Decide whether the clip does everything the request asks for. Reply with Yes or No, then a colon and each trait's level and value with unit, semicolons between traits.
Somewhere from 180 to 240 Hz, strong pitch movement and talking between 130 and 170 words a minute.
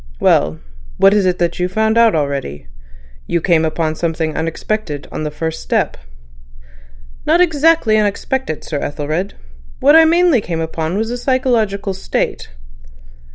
Yes: medium, 185 Hz; wide, 6.5 semitones; average, 145 wpm